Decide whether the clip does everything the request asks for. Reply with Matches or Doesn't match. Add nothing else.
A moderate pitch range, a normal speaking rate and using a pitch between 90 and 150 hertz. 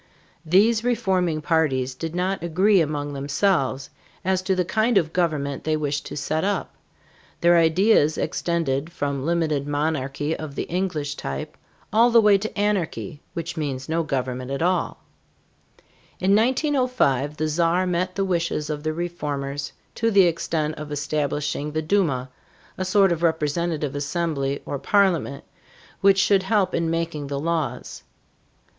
Doesn't match